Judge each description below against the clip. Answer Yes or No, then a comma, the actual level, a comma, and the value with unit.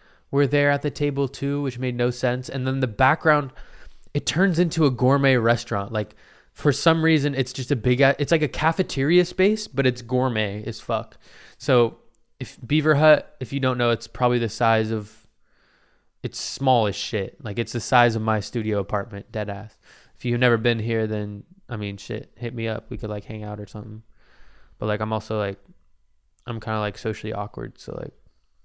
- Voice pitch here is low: Yes, low, 120 Hz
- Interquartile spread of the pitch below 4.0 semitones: No, average, 4.3 semitones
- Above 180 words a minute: Yes, average, 200 wpm